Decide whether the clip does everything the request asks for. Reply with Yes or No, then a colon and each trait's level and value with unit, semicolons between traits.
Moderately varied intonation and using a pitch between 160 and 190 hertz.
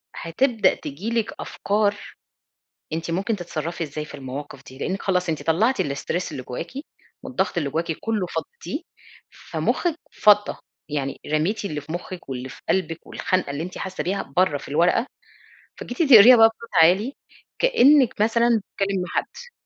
No: wide, 6.3 semitones; medium, 185 Hz